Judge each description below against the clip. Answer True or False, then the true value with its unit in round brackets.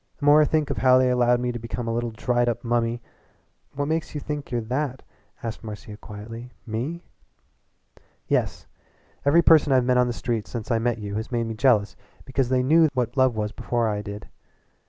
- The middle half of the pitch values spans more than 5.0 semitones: False (2.6 semitones)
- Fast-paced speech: True (210 wpm)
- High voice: False (120 Hz)